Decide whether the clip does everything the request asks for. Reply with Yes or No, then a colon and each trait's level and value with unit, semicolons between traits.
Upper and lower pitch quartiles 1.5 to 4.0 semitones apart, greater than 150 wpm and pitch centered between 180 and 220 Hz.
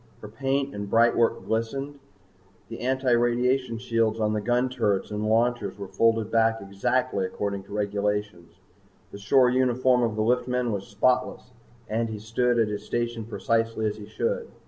No: average, 2.9 semitones; average, 160 wpm; low, 115 Hz